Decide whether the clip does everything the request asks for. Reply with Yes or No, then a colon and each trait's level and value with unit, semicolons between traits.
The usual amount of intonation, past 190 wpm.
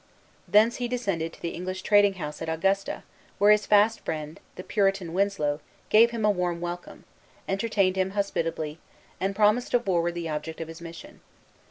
No: average, 3.8 semitones; average, 175 wpm